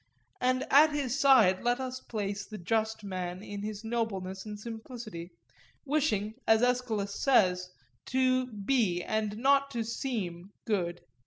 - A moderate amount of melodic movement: Yes, average, 4.3 semitones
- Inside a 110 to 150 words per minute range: Yes, average, 140 wpm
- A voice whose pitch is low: No, high, 220 Hz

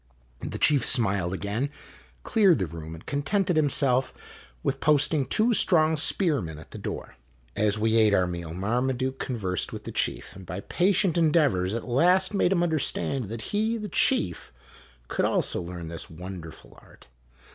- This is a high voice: No, low, 125 Hz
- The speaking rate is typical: Yes, average, 165 wpm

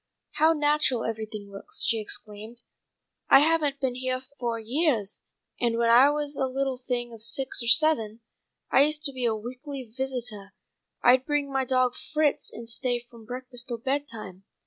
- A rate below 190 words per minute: Yes, average, 170 wpm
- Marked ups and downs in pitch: No, average, 3.3 semitones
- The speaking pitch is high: Yes, very high, 250 Hz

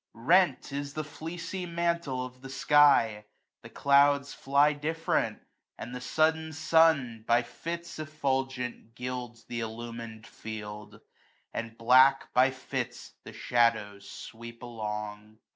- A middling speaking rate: No, slow, 125 wpm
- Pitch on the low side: Yes, low, 130 Hz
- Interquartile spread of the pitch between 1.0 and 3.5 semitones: No, average, 4.5 semitones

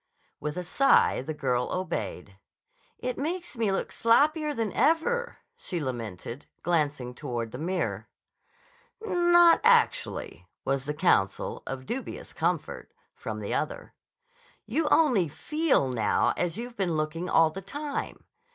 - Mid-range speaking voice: Yes, medium, 180 Hz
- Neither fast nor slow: No, slow, 125 wpm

